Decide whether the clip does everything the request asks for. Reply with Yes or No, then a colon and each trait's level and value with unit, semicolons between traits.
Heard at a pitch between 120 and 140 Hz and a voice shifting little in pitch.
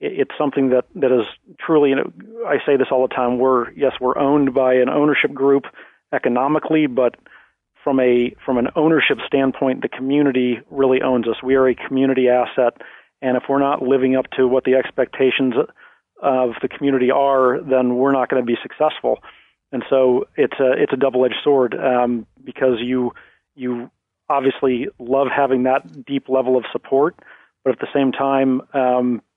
Yes: low, 130 Hz; narrow, 1.5 semitones